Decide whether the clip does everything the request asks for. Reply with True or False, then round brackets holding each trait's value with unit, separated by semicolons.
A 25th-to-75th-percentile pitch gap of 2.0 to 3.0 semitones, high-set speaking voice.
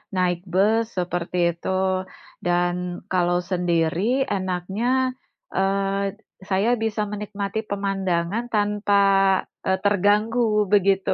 True (2.5 semitones; 195 Hz)